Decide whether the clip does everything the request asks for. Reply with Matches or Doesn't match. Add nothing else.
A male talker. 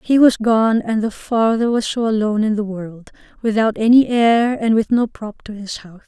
Doesn't match